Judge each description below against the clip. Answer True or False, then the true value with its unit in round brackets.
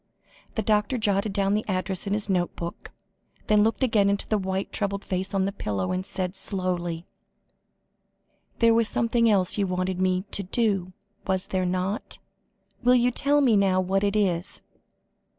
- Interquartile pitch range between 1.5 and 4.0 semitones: True (2.4 semitones)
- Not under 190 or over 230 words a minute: False (170 wpm)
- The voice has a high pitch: True (195 Hz)